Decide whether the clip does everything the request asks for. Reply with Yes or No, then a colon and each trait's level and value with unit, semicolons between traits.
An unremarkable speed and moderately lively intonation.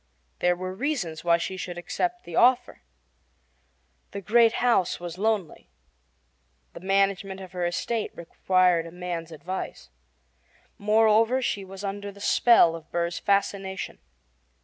No: slow, 130 wpm; average, 3.3 semitones